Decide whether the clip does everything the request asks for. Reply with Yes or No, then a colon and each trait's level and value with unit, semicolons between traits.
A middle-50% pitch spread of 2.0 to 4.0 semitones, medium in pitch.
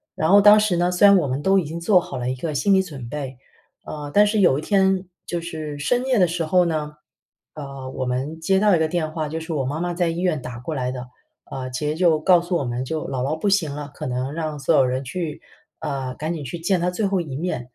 No: average, 4.6 semitones; medium, 160 Hz